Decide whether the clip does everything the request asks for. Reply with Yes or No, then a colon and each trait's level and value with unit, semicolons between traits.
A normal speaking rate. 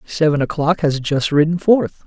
Yes: average, 175 wpm